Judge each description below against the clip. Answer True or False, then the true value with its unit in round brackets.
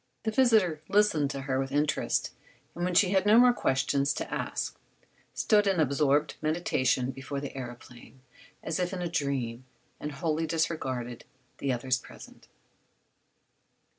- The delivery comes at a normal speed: True (145 wpm)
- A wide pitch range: False (5.0 semitones)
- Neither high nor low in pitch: True (150 Hz)